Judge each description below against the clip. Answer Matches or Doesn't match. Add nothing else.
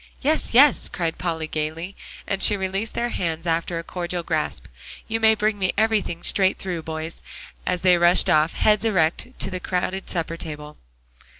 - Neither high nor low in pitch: Matches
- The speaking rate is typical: Matches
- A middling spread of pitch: Matches